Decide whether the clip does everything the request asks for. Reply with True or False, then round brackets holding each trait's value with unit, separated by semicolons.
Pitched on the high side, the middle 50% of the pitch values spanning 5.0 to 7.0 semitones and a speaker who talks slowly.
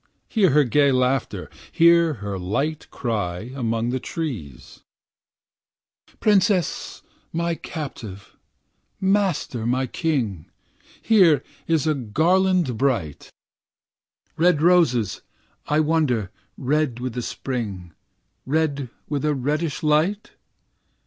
False (140 Hz; 5.6 semitones; 100 wpm)